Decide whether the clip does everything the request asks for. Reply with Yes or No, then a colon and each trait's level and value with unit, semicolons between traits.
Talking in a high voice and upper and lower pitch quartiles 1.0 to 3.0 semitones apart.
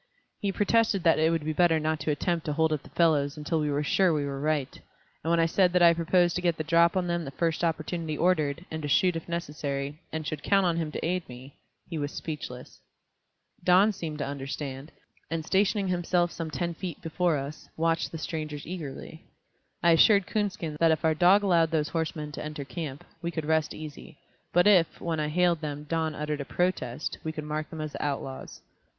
No: medium, 160 Hz; narrow, 2.5 semitones